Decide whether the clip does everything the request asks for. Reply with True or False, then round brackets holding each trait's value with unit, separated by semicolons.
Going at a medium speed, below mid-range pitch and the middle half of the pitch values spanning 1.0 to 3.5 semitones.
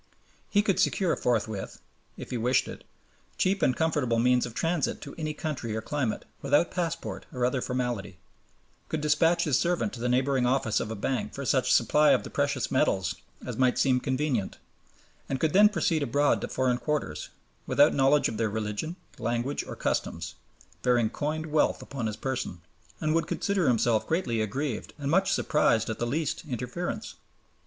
False (175 wpm; 130 Hz; 4.6 semitones)